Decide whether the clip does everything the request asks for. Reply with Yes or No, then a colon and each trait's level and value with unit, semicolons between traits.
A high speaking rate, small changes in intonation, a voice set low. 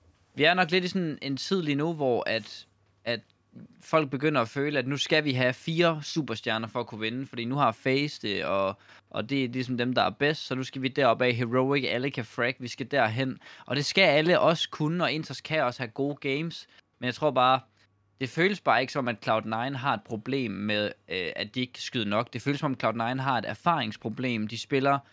No: fast, 235 wpm; average, 3.7 semitones; low, 130 Hz